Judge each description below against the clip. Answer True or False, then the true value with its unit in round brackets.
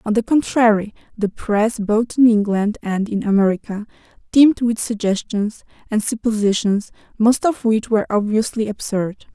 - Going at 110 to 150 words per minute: True (140 wpm)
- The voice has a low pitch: False (220 Hz)